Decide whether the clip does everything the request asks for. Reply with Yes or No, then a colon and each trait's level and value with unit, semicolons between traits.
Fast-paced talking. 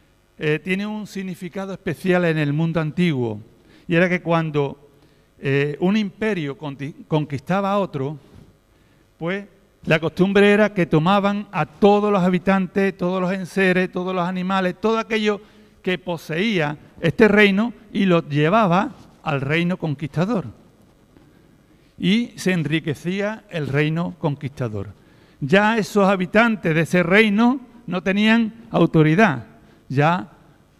No: slow, 125 wpm